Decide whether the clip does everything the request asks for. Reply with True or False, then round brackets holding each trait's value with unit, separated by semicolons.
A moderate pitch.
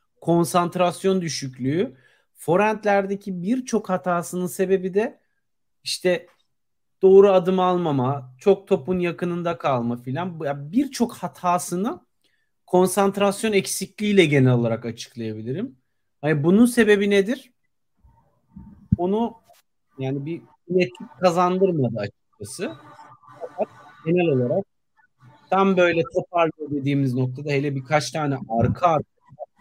True (175 Hz)